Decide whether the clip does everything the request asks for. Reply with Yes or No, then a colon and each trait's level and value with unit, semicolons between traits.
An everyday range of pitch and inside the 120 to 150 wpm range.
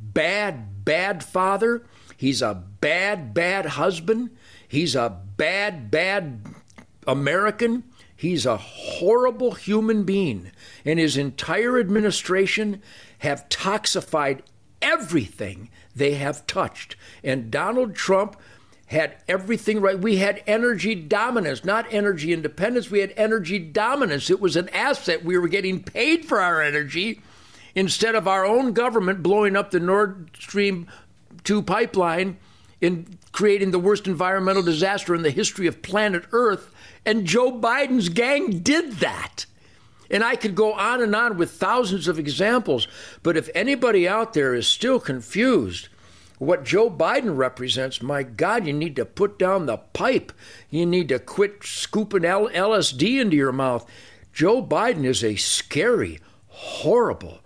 No: wide, 6.3 semitones; average, 140 wpm